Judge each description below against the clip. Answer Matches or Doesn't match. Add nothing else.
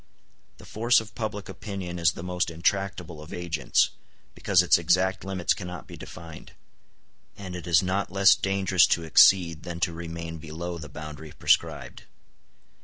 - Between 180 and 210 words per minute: Doesn't match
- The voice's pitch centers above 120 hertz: Doesn't match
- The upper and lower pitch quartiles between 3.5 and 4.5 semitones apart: Doesn't match